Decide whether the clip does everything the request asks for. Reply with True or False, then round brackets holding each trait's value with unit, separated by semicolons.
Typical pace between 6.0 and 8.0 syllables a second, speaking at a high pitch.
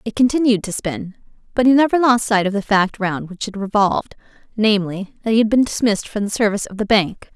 True (6.1 syllables/s; 210 Hz)